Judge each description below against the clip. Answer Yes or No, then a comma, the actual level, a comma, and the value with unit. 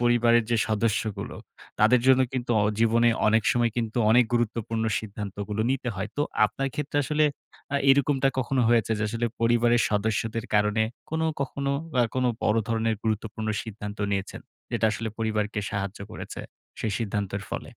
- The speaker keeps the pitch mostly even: Yes, narrow, 2.1 semitones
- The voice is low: Yes, low, 115 Hz